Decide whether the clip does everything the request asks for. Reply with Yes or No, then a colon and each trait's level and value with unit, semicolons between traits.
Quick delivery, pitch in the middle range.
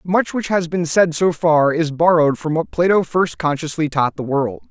Yes: fast, 215 wpm; medium, 160 Hz